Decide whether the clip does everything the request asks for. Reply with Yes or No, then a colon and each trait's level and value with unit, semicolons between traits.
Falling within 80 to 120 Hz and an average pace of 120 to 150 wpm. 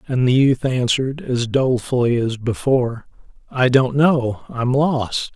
No: low, 130 Hz; average, 145 wpm